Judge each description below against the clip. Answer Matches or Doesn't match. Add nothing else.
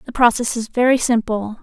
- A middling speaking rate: Matches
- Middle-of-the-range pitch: Doesn't match